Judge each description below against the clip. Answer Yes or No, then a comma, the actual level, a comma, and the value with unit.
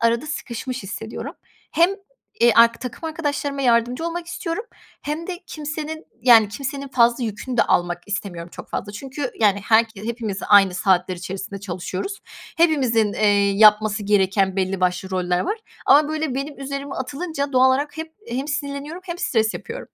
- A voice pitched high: Yes, high, 235 Hz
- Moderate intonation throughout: No, wide, 6.1 semitones